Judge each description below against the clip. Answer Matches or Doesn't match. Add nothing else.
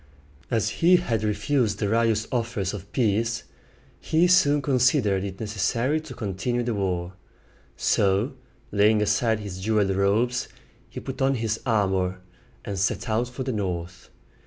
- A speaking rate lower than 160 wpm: Matches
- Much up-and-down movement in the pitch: Doesn't match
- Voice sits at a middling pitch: Doesn't match